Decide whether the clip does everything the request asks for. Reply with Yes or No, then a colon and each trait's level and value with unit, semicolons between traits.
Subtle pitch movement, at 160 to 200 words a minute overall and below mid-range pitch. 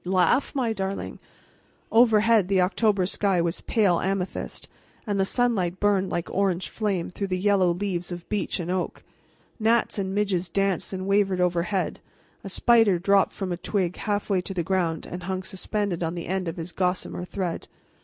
No: narrow, 2.2 semitones; average, 175 wpm; high, 190 Hz